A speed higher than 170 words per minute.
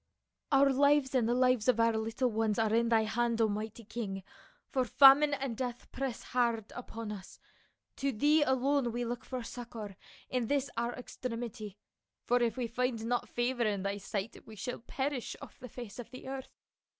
Yes: average, 190 wpm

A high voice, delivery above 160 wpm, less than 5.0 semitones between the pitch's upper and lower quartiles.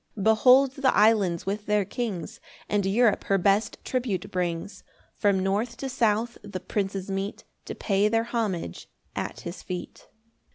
No: high, 205 Hz; average, 155 wpm; average, 3.0 semitones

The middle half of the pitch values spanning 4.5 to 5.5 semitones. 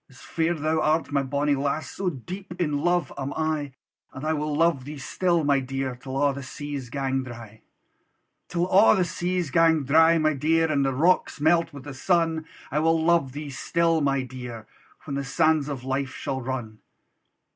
No: average, 3.3 semitones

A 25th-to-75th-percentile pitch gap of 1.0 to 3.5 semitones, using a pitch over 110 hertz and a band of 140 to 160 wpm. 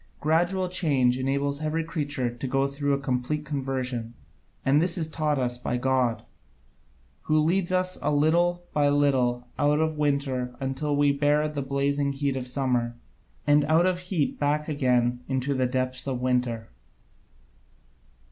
Yes: average, 2.9 semitones; medium, 140 Hz; average, 155 wpm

